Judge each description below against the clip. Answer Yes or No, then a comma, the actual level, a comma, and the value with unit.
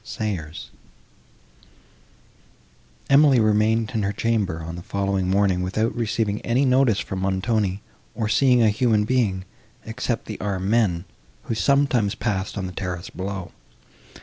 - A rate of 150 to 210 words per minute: No, slow, 135 wpm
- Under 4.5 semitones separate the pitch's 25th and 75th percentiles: Yes, average, 3.4 semitones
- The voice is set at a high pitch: No, low, 105 Hz